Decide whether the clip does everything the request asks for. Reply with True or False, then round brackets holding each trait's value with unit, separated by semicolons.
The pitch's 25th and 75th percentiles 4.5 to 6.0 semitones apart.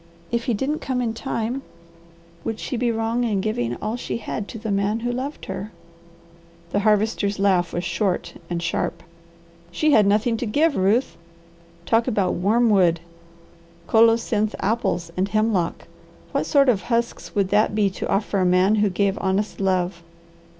False (3.4 semitones)